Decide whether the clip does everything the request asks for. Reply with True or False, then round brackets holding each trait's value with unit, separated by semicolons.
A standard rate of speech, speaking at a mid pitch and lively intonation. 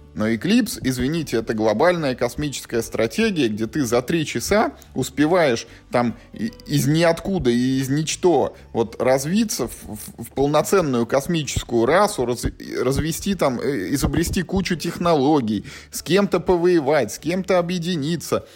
True (125 wpm; 145 Hz; 6.7 semitones)